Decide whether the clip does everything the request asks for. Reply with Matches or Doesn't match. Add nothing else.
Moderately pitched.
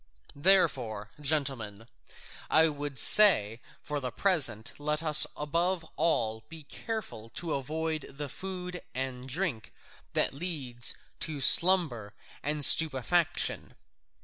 Matches